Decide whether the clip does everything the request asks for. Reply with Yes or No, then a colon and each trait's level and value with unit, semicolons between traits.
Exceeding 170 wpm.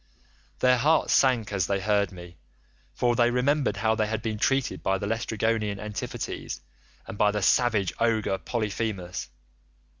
No: average, 150 wpm